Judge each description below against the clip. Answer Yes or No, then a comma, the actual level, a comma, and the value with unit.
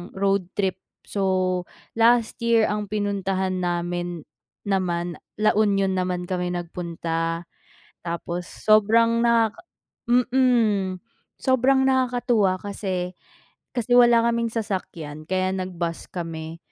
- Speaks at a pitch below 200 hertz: Yes, high, 190 Hz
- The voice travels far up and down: No, average, 4.5 semitones